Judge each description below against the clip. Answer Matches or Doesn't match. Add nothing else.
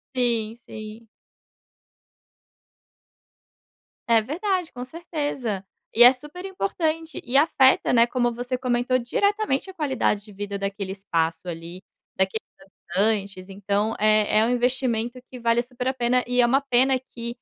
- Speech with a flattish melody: Doesn't match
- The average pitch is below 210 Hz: Doesn't match